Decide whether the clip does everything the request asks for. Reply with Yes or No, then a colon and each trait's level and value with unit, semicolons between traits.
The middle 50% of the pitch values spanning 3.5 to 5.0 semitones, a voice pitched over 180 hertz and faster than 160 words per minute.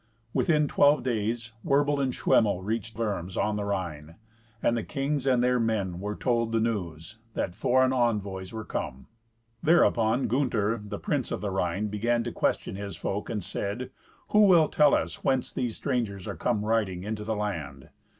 No: average, 3.9 semitones; low, 110 Hz; average, 175 wpm